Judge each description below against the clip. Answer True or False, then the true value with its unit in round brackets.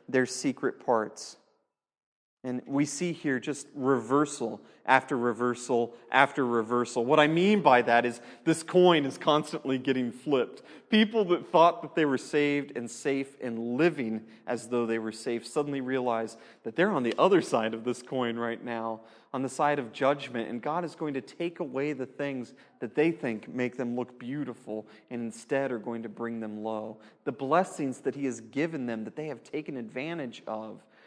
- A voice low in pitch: True (130 Hz)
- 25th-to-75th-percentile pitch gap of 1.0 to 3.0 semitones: False (3.8 semitones)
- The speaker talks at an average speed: True (185 wpm)